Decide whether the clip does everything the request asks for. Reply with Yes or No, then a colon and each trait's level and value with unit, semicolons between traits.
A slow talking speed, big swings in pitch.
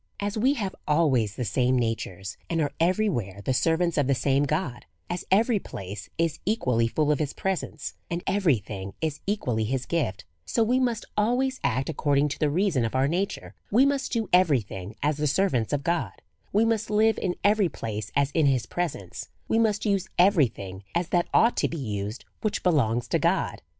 No: average, 200 wpm; wide, 8.4 semitones